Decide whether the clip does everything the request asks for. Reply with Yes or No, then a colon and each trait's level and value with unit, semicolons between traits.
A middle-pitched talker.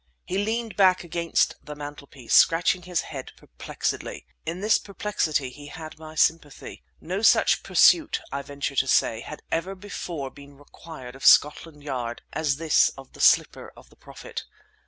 Yes: medium, 155 Hz